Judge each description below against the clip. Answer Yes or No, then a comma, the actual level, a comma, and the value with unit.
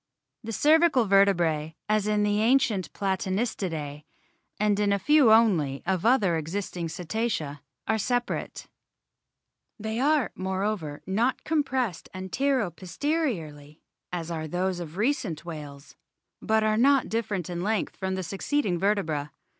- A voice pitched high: Yes, high, 195 Hz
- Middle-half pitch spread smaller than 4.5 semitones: No, average, 5.0 semitones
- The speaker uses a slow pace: Yes, slow, 130 wpm